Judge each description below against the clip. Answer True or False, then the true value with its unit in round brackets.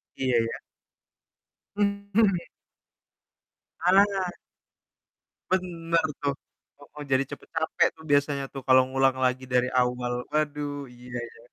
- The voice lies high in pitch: False (145 Hz)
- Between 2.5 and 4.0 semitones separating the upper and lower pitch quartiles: False (5.0 semitones)